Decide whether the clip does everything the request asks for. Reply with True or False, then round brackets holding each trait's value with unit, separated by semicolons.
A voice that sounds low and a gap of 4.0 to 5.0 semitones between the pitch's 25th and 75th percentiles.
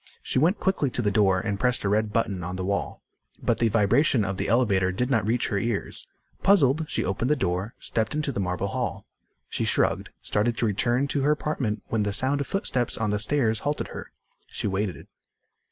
True (115 Hz; 4.7 semitones)